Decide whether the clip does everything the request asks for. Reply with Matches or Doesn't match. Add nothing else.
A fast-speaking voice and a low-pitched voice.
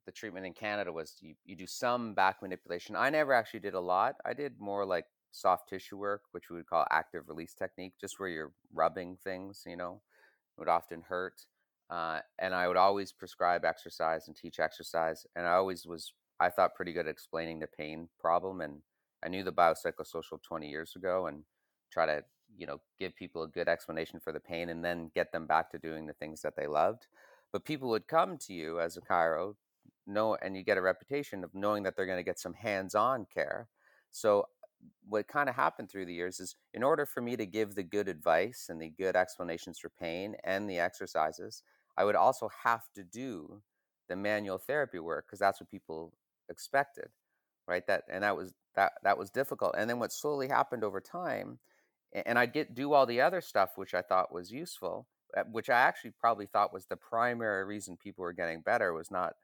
Matches